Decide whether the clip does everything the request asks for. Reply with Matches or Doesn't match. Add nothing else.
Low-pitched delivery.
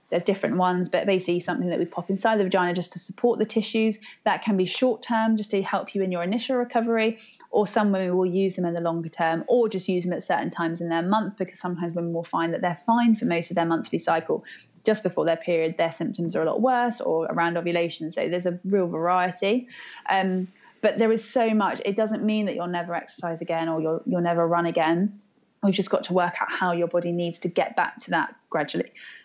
Doesn't match